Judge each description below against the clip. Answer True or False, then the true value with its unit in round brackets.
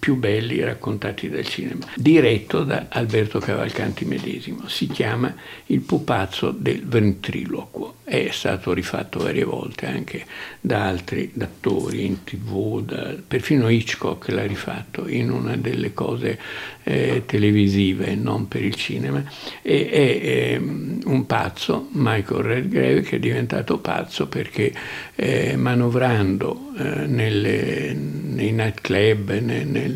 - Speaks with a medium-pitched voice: False (105 Hz)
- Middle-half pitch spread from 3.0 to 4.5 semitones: False (2.6 semitones)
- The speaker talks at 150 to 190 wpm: False (125 wpm)